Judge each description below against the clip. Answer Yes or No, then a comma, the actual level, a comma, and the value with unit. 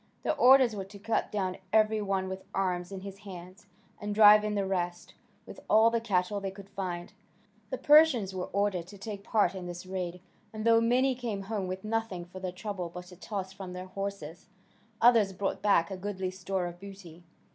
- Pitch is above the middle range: Yes, high, 195 Hz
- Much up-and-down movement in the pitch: No, narrow, 2.6 semitones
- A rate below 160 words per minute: No, average, 200 wpm